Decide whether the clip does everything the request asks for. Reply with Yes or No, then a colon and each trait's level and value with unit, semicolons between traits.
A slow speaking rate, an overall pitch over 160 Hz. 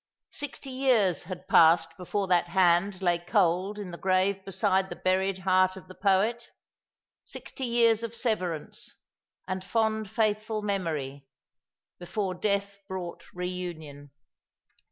Yes: slow, 125 wpm; high, 190 Hz